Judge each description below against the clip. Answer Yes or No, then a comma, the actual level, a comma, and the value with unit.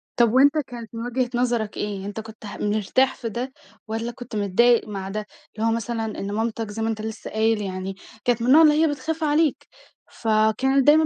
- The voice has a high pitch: Yes, high, 225 Hz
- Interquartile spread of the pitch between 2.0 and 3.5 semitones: Yes, average, 3.0 semitones